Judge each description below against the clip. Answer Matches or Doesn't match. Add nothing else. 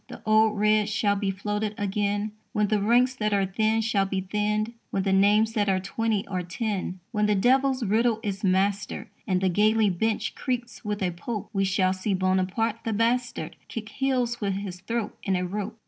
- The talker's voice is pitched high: Matches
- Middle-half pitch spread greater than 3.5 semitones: Doesn't match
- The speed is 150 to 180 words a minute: Doesn't match